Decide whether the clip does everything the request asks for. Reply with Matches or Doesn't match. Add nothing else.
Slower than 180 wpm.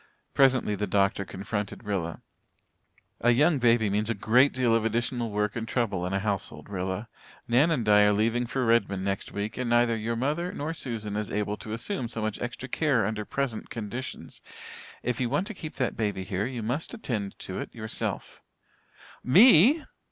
Doesn't match